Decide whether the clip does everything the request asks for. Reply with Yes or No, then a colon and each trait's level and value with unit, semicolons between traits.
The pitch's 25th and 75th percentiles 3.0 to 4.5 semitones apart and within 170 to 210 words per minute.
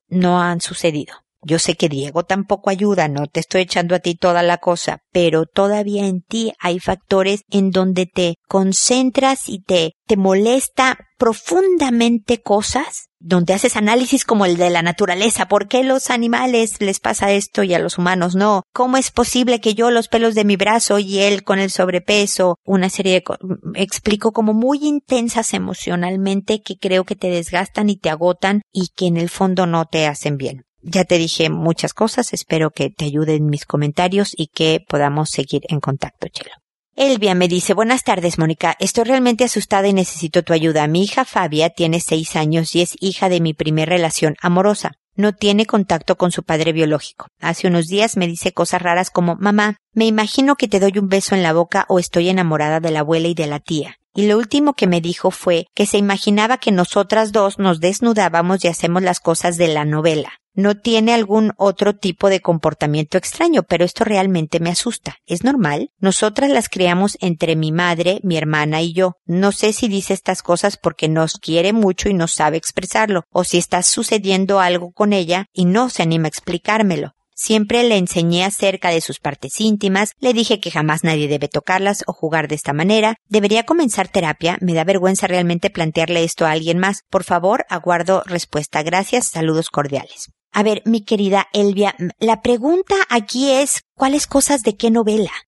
Yes: average, 3.8 semitones; fast, 190 wpm